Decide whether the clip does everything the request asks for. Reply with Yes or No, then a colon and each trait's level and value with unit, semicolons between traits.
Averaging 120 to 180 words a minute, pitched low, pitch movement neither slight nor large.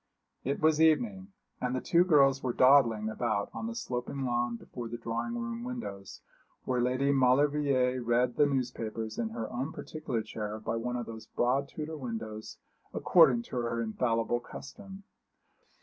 Yes: average, 160 wpm; low, 125 Hz; average, 3.9 semitones